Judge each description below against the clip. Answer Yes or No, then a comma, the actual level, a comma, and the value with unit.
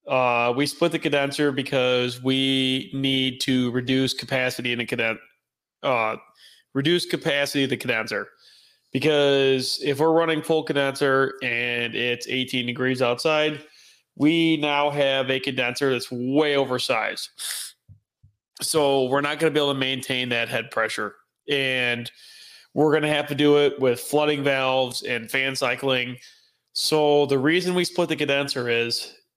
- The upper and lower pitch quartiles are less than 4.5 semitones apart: Yes, narrow, 2.6 semitones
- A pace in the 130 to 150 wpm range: Yes, average, 145 wpm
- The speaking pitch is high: No, low, 135 Hz